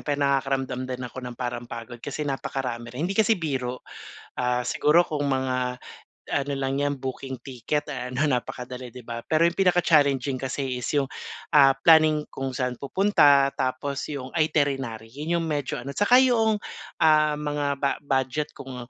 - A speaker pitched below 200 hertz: Yes, low, 135 Hz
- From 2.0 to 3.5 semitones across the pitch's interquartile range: Yes, average, 2.9 semitones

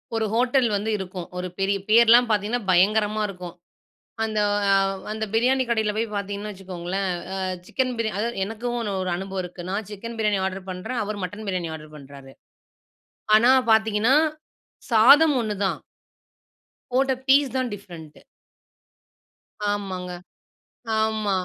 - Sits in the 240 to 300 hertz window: No, high, 210 Hz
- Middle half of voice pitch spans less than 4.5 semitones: Yes, average, 3.2 semitones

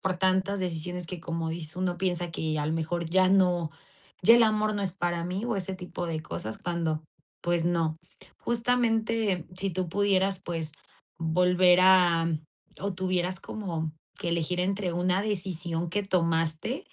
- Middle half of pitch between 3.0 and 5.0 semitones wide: No, narrow, 2.4 semitones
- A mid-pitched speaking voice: Yes, medium, 180 Hz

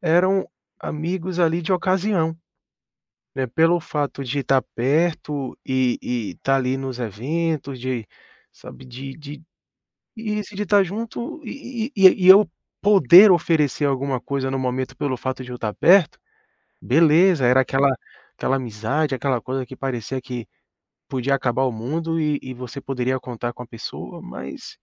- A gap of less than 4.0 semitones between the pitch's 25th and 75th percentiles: No, average, 5.0 semitones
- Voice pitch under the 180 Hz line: Yes, medium, 140 Hz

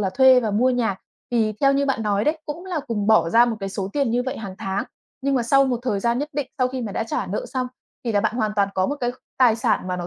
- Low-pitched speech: No, high, 235 Hz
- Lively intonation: No, average, 4.2 semitones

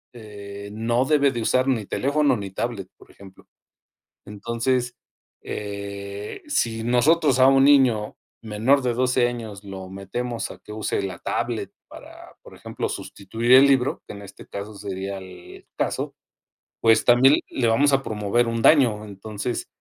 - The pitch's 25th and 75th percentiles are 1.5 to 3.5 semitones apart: No, average, 4.0 semitones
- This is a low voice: Yes, low, 115 Hz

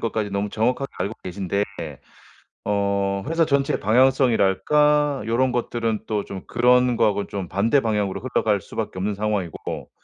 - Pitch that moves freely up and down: No, average, 4.0 semitones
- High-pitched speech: No, low, 110 Hz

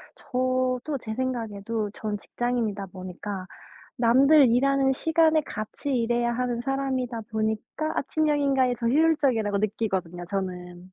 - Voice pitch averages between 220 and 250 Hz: Yes, high, 240 Hz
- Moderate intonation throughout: Yes, average, 4.5 semitones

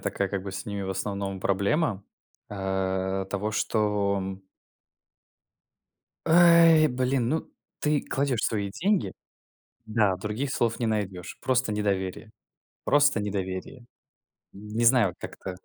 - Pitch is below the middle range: Yes, low, 105 Hz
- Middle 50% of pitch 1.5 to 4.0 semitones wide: No, average, 4.6 semitones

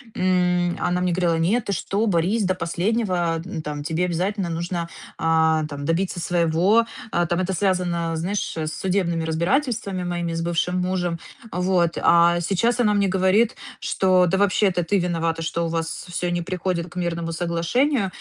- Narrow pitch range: Yes, narrow, 2.3 semitones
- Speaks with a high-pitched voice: No, medium, 175 Hz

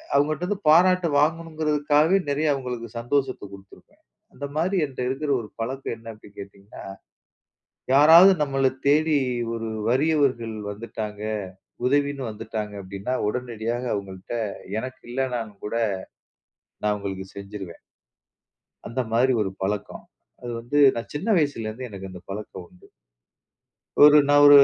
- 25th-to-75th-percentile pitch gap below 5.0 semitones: No, wide, 5.6 semitones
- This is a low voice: Yes, low, 125 Hz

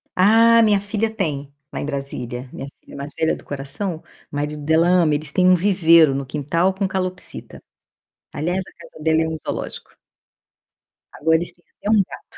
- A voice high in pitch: No, medium, 160 Hz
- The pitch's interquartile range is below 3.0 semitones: No, average, 4.5 semitones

